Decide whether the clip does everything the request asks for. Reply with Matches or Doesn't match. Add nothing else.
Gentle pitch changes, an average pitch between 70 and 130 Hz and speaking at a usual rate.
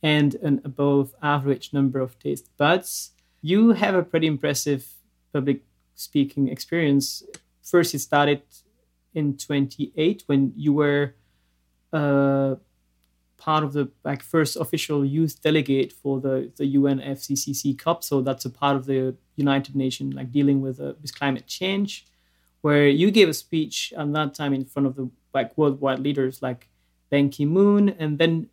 Doesn't match